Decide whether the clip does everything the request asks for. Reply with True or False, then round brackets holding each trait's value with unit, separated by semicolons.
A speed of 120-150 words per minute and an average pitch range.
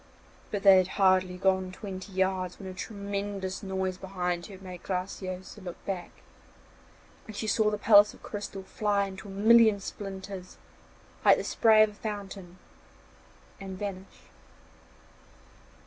False (140 wpm; 1.6 semitones)